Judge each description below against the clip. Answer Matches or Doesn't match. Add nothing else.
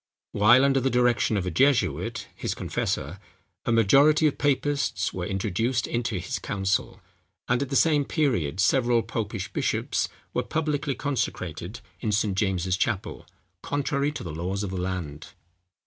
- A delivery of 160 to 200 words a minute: Doesn't match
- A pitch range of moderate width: Doesn't match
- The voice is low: Matches